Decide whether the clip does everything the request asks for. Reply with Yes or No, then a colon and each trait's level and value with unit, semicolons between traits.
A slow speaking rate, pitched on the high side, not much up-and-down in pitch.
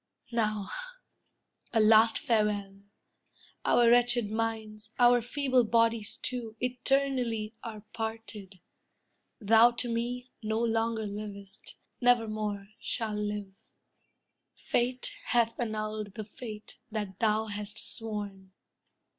Yes: slow, 100 wpm; high, 220 Hz; narrow, 2.1 semitones